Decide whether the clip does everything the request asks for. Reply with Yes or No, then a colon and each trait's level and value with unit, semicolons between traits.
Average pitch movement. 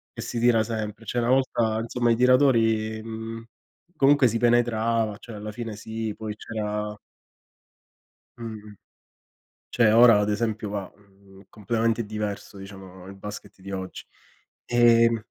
No: narrow, 1.9 semitones